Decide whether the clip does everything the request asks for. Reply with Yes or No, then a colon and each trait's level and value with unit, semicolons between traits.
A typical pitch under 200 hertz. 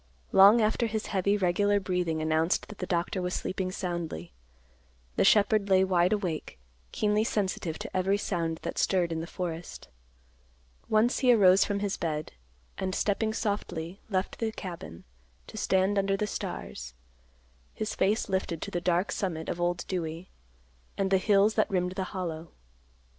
Yes: medium, 185 Hz